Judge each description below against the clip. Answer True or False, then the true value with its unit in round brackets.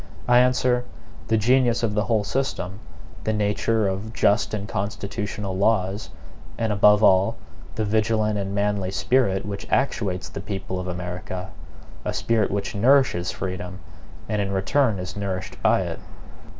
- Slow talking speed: False (150 wpm)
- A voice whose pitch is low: True (105 Hz)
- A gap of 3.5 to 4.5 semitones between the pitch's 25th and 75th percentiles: False (2.7 semitones)